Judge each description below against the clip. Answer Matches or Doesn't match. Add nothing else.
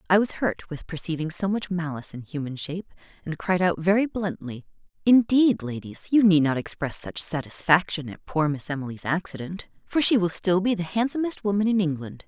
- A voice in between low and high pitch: Matches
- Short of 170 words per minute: Doesn't match